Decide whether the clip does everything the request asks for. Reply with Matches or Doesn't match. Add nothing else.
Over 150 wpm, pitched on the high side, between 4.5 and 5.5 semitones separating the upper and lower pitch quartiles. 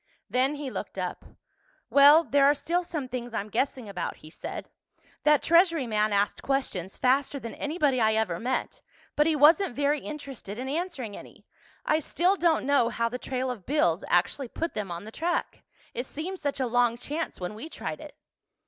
Matches